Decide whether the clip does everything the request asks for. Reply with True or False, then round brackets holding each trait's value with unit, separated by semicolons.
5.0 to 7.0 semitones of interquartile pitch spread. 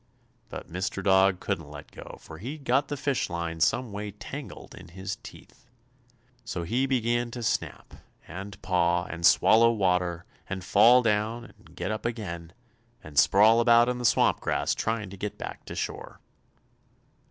False (4.6 semitones)